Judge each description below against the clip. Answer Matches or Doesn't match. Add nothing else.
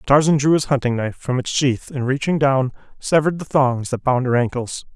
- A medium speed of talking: Doesn't match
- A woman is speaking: Doesn't match